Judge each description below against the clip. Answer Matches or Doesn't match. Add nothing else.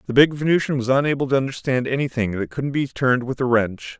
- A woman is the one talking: Doesn't match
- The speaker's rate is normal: Doesn't match